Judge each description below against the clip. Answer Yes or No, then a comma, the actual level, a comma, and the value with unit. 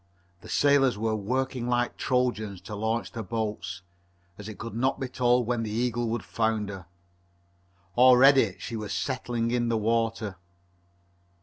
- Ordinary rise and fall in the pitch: No, narrow, 2.3 semitones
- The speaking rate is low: No, average, 145 wpm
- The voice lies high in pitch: No, low, 115 Hz